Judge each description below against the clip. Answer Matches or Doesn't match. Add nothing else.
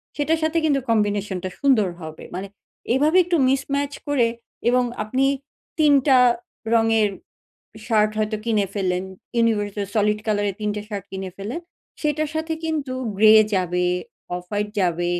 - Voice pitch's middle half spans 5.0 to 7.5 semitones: Matches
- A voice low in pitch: Doesn't match